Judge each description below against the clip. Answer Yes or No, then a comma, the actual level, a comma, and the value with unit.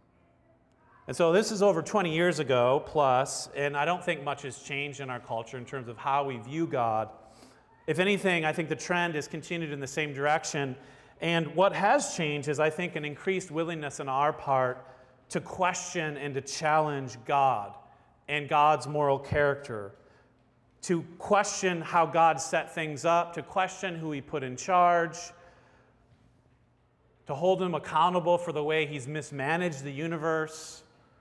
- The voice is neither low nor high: Yes, medium, 150 Hz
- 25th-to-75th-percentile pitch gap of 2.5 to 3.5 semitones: No, average, 4.0 semitones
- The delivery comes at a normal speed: Yes, average, 165 wpm